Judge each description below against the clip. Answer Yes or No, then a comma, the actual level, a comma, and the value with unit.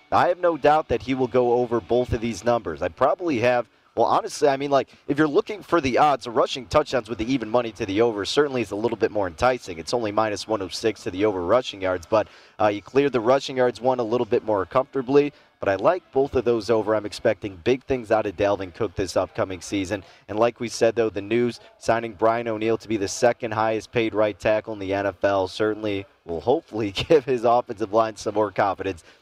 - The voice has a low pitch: Yes, low, 115 Hz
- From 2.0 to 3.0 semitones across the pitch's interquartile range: Yes, average, 2.7 semitones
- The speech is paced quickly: Yes, fast, 235 wpm